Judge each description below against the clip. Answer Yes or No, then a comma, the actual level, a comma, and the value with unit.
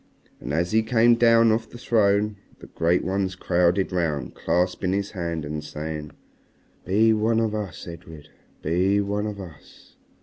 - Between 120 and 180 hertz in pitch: No, very low, 95 Hz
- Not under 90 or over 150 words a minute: No, average, 165 wpm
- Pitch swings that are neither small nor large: Yes, average, 4.2 semitones